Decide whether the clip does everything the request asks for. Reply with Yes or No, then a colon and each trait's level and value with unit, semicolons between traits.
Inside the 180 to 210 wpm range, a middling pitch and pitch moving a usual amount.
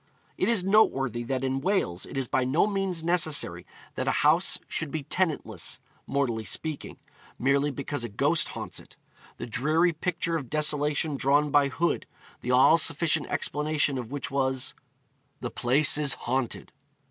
No: average, 160 wpm; medium, 145 Hz; average, 3.4 semitones